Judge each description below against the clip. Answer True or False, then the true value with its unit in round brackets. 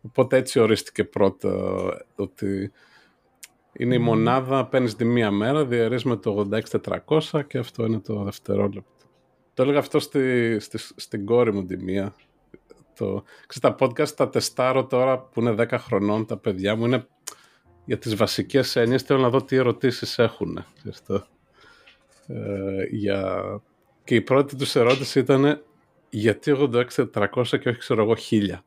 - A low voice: True (120 Hz)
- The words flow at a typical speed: True (150 wpm)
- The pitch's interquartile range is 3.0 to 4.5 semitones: True (4.0 semitones)